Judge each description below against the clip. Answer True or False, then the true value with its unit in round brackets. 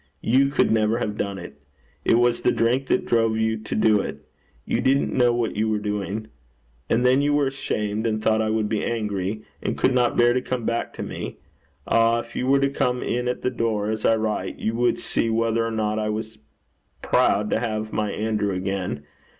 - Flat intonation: True (2.1 semitones)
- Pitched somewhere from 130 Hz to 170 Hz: False (110 Hz)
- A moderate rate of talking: False (215 wpm)